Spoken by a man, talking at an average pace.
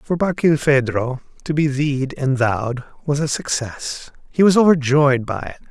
Yes: male; average, 160 wpm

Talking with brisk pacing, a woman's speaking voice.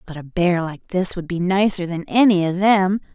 Yes: fast, 230 wpm; female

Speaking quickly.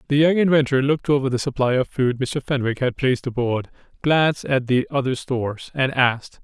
No: average, 195 wpm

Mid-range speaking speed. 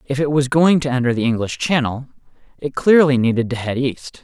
No: fast, 215 wpm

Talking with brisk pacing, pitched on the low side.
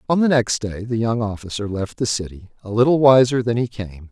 Yes: fast, 235 wpm; low, 115 Hz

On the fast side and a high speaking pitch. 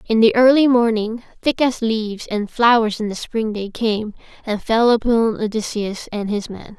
No: average, 185 wpm; high, 225 Hz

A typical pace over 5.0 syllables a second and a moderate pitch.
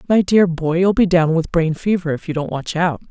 Yes: 5.3 syllables/s; medium, 170 Hz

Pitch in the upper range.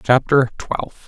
No: low, 125 Hz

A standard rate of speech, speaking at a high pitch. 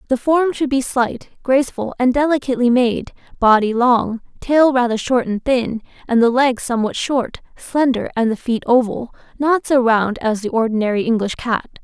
Yes: average, 170 wpm; high, 245 Hz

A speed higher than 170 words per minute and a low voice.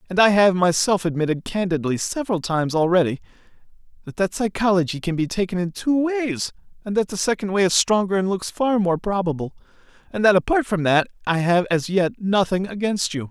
No: average, 190 wpm; medium, 185 Hz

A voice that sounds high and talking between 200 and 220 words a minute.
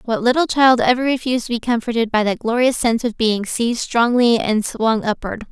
Yes: high, 235 Hz; fast, 205 wpm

